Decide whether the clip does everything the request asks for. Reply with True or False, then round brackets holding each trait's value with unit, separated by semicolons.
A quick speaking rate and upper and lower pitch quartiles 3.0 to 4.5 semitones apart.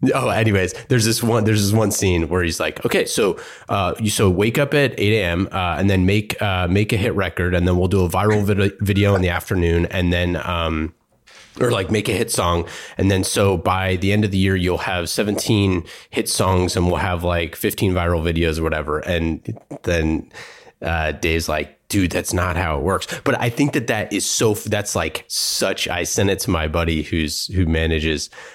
True (220 wpm; 3.3 semitones)